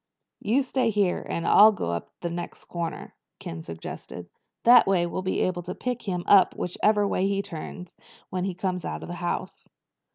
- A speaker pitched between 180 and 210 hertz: Yes, medium, 185 Hz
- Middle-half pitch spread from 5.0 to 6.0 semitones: No, average, 2.9 semitones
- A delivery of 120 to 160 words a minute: No, average, 195 wpm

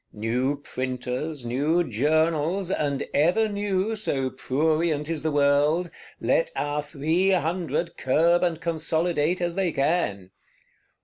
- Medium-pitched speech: Yes, medium, 160 Hz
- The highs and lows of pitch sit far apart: No, average, 3.5 semitones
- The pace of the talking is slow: Yes, slow, 120 wpm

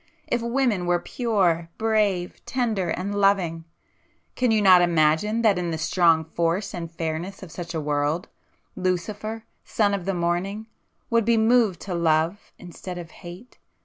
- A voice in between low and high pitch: Yes, medium, 180 Hz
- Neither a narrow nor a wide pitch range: Yes, average, 4.0 semitones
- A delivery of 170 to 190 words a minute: No, average, 150 wpm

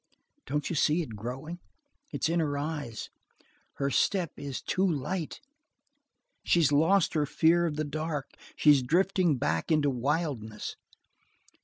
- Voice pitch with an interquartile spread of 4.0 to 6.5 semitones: No, average, 3.3 semitones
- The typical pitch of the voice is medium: Yes, medium, 150 Hz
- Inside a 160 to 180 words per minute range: No, slow, 135 wpm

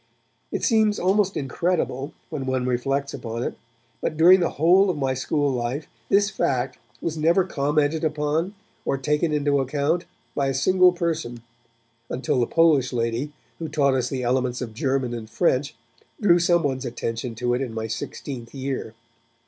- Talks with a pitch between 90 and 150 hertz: Yes, medium, 140 Hz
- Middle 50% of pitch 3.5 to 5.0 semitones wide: Yes, average, 4.6 semitones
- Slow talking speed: No, average, 165 wpm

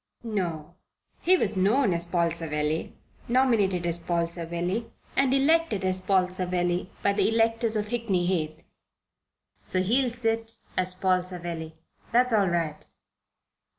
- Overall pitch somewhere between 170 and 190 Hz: Yes, medium, 185 Hz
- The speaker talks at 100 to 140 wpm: Yes, slow, 135 wpm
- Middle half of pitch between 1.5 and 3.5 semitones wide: No, average, 4.8 semitones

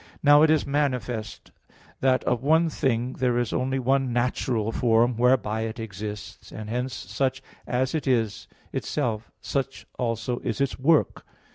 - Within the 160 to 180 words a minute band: No, average, 150 wpm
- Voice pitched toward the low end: Yes, low, 125 Hz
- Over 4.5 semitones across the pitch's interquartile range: No, average, 2.8 semitones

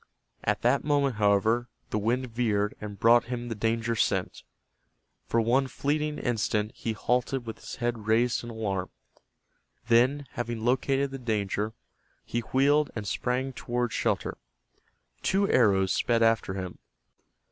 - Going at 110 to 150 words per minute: Yes, average, 140 wpm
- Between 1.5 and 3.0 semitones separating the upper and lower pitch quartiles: Yes, average, 2.7 semitones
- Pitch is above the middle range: No, low, 120 Hz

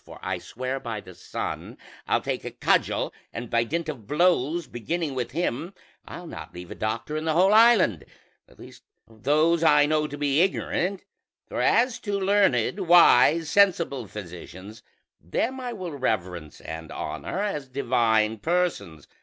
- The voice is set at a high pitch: No, medium, 145 Hz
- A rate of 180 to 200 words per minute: No, average, 160 wpm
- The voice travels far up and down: Yes, wide, 7.9 semitones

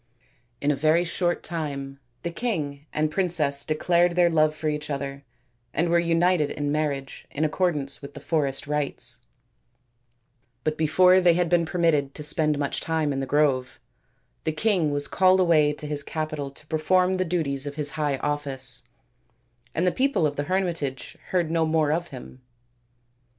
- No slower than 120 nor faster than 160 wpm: No, average, 170 wpm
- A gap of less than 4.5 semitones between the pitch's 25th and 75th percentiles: Yes, average, 3.0 semitones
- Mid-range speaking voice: Yes, medium, 155 Hz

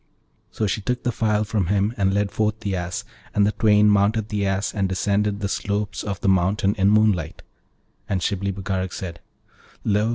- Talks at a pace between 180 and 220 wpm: Yes, average, 190 wpm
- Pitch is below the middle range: Yes, low, 100 Hz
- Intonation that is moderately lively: No, narrow, 1.5 semitones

